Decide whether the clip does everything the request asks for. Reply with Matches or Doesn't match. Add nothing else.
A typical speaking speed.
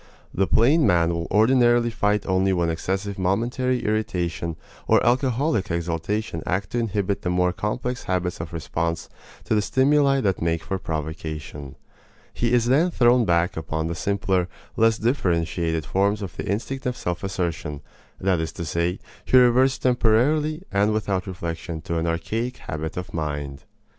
Matches